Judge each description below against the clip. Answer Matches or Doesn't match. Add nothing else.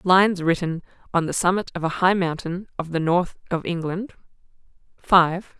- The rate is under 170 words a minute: Matches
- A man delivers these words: Doesn't match